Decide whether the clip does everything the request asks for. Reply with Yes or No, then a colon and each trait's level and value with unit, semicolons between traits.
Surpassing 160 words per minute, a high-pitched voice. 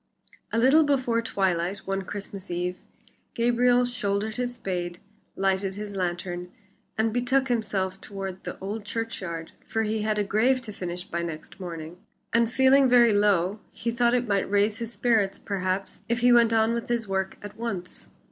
Yes: average, 170 wpm; high, 210 Hz